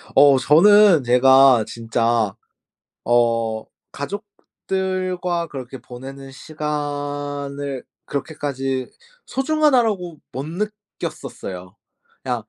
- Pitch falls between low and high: Yes, medium, 145 Hz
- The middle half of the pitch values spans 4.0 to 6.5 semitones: Yes, wide, 5.8 semitones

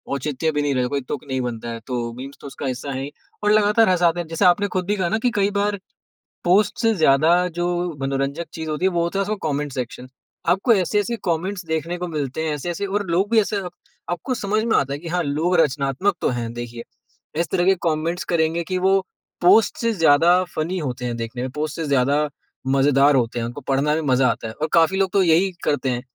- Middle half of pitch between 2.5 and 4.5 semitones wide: No, average, 5.3 semitones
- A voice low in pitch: No, medium, 160 Hz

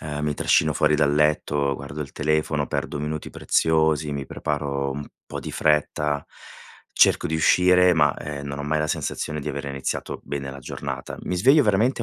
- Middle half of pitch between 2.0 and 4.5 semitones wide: No, narrow, 1.5 semitones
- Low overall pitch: Yes, very low, 75 Hz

